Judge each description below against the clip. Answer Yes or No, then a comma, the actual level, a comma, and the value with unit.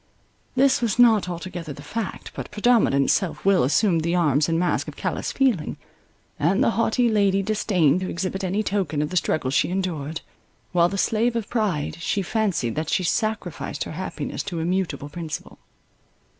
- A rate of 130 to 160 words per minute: No, average, 170 wpm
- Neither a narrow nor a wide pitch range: Yes, average, 4.7 semitones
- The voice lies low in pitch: No, medium, 185 Hz